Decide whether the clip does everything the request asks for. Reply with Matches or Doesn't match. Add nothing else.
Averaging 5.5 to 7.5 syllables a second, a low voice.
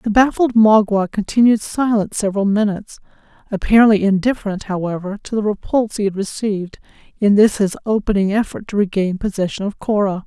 Doesn't match